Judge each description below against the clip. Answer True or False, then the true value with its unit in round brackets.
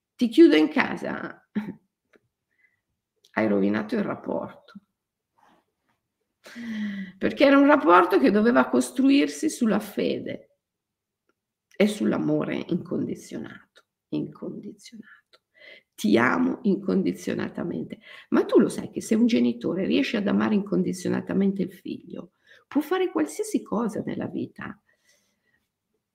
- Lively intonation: True (7.0 semitones)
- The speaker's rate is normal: False (100 wpm)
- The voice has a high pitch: True (210 Hz)